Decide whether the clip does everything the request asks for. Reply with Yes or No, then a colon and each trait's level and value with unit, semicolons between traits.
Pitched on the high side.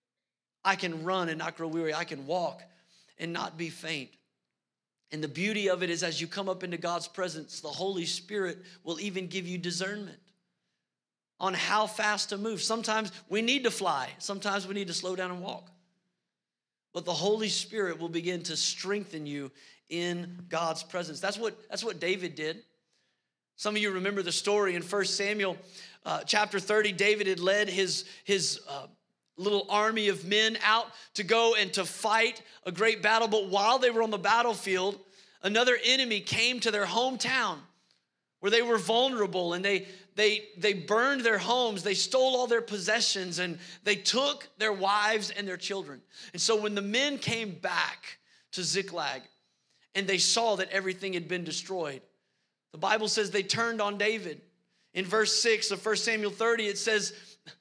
Yes: high, 195 Hz